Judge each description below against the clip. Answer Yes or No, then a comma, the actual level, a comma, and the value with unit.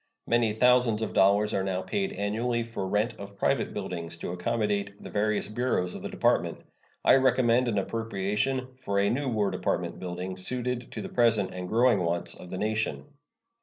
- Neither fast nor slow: Yes, average, 180 wpm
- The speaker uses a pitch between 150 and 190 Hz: No, low, 105 Hz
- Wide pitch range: No, average, 3.8 semitones